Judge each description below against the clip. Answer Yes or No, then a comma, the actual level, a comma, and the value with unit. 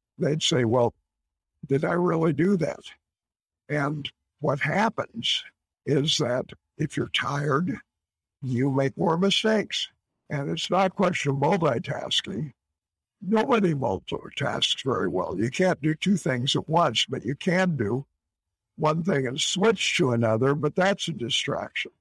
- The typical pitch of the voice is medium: Yes, medium, 145 Hz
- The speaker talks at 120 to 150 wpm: Yes, average, 140 wpm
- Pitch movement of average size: No, wide, 7.2 semitones